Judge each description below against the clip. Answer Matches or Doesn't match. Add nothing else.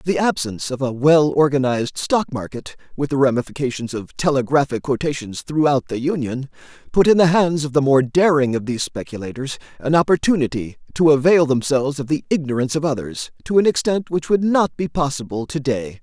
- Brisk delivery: Doesn't match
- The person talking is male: Matches